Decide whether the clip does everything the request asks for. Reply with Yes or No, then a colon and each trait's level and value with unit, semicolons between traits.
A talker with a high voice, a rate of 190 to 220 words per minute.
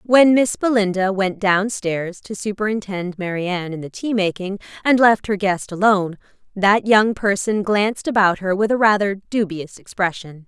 No: high, 200 Hz; average, 170 wpm